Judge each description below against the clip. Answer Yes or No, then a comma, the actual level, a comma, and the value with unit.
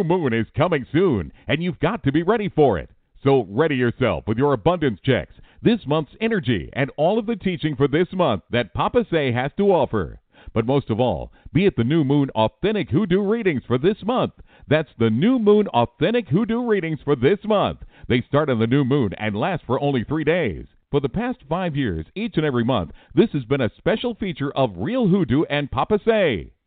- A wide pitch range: Yes, wide, 7.3 semitones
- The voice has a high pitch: No, medium, 145 Hz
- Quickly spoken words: Yes, fast, 210 wpm